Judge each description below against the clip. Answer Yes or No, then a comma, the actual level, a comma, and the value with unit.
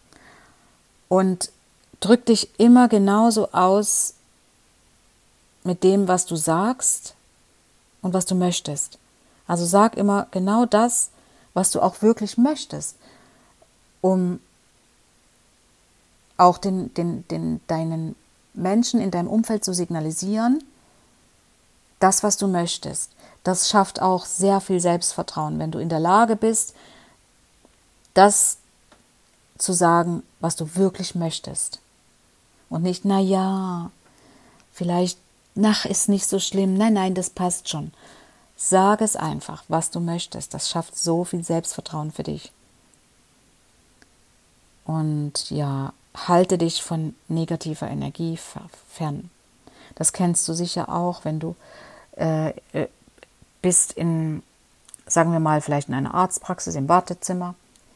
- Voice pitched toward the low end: No, medium, 180 Hz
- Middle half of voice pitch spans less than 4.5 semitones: Yes, average, 3.2 semitones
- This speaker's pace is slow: Yes, slow, 120 wpm